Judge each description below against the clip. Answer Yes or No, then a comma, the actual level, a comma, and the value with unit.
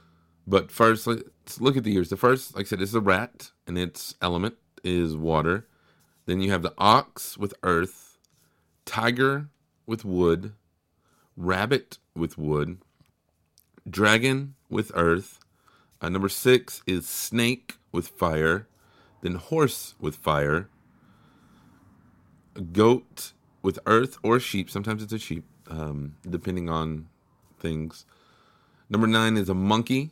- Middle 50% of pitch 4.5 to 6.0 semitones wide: Yes, average, 5.3 semitones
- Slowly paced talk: Yes, slow, 130 wpm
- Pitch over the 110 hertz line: No, very low, 95 Hz